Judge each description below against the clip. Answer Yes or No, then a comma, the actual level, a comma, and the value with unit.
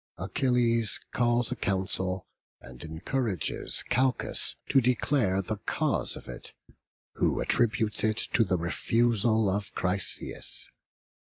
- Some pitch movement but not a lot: Yes, average, 4.1 semitones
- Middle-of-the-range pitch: No, low, 110 Hz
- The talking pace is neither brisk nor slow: No, slow, 110 wpm